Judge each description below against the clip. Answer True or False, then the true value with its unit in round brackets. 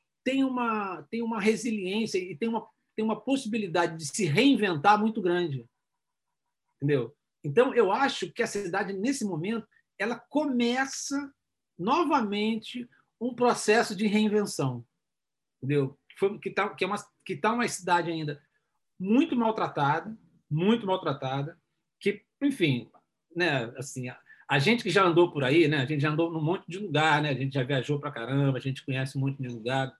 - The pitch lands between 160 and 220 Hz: True (190 Hz)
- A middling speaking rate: True (165 wpm)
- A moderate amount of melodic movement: False (7.1 semitones)